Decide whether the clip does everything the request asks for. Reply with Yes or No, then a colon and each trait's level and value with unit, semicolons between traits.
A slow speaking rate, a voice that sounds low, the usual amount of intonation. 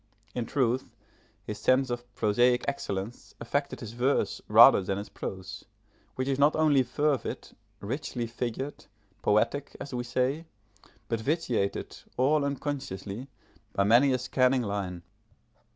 Yes: slow, 130 wpm; low, 125 Hz; average, 4.0 semitones